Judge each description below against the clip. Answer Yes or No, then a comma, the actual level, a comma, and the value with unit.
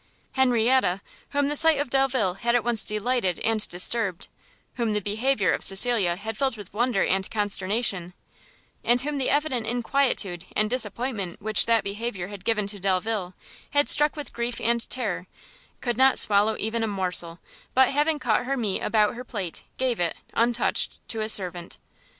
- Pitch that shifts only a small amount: No, average, 4.1 semitones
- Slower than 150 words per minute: No, average, 170 wpm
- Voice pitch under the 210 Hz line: No, high, 225 Hz